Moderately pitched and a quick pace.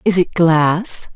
No: medium, 175 Hz; average, 155 wpm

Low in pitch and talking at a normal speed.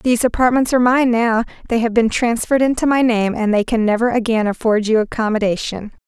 No: high, 230 Hz; average, 195 wpm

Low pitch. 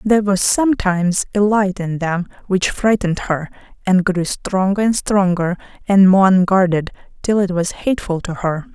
No: high, 190 Hz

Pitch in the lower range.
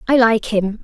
No: high, 225 Hz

